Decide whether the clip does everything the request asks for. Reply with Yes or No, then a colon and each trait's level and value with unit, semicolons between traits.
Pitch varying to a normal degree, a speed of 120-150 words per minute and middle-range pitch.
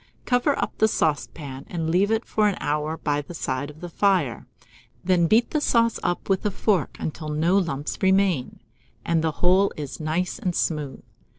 No: average, 4.7 semitones; average, 185 wpm; medium, 170 Hz